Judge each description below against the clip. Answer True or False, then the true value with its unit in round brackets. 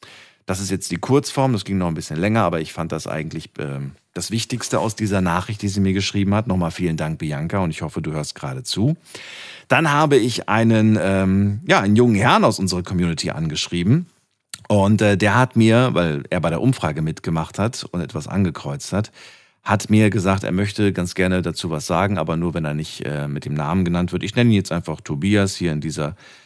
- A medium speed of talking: False (220 wpm)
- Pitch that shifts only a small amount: False (4.4 semitones)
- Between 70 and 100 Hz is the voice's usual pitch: True (95 Hz)